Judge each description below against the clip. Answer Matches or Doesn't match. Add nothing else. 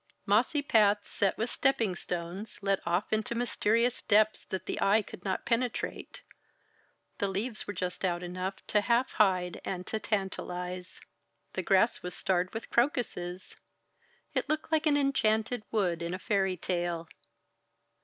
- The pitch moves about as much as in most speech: Matches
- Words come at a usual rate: Matches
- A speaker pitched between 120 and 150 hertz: Doesn't match